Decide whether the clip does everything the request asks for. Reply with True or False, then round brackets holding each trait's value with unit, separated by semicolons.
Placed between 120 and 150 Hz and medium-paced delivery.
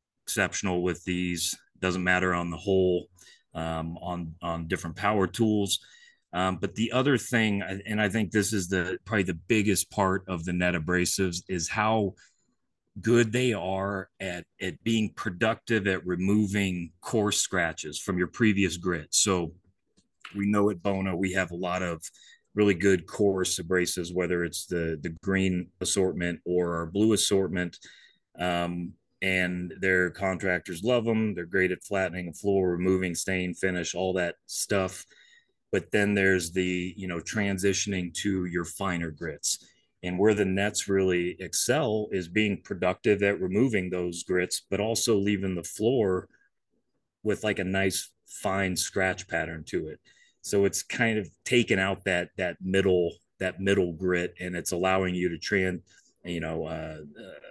False (95 Hz; 160 wpm)